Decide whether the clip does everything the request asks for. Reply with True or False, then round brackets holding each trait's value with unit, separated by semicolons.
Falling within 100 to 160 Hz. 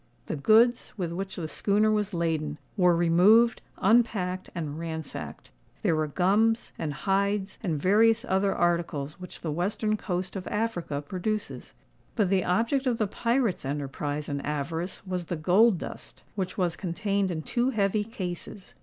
False (185 Hz)